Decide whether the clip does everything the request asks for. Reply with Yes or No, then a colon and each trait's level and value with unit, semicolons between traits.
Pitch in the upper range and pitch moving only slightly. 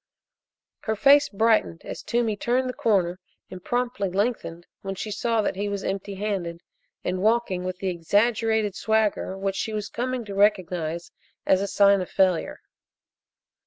No: high, 200 Hz; average, 3.2 semitones